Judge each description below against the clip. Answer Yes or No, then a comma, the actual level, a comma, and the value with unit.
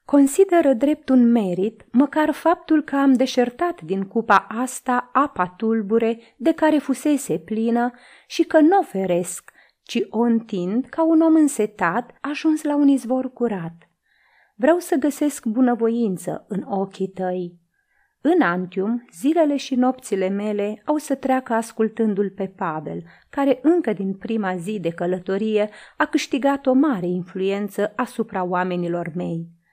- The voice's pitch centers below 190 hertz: No, high, 235 Hz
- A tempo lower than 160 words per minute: Yes, average, 140 wpm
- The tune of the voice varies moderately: No, wide, 6.5 semitones